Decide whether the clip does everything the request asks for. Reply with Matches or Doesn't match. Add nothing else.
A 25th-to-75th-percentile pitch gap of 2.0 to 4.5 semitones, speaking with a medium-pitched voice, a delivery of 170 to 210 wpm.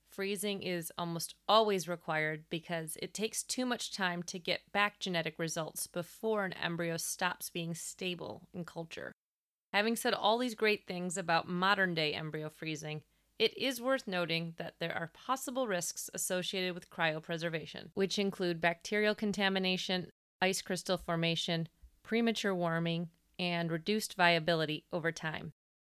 Doesn't match